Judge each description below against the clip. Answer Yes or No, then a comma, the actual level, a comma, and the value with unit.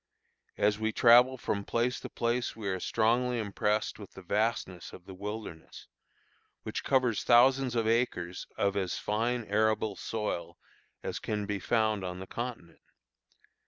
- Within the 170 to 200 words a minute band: No, average, 150 wpm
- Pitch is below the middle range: Yes, low, 110 Hz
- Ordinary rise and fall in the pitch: Yes, average, 3.0 semitones